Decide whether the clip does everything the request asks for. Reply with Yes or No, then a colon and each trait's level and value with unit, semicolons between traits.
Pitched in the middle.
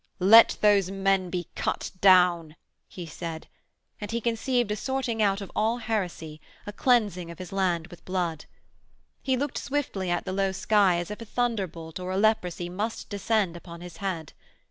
No: high, 195 Hz